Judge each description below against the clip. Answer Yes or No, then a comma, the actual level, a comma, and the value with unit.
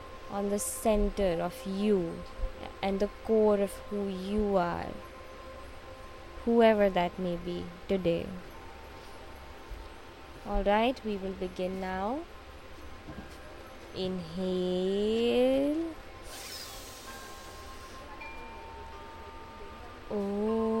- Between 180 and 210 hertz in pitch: Yes, high, 190 Hz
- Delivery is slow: Yes, slow, 70 wpm